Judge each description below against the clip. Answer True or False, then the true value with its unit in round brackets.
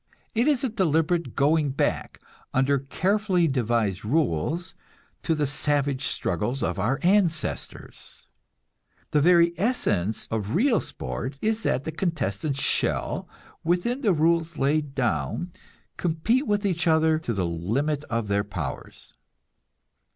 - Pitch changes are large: True (6.5 semitones)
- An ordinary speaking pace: False (130 wpm)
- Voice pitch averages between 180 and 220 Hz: False (155 Hz)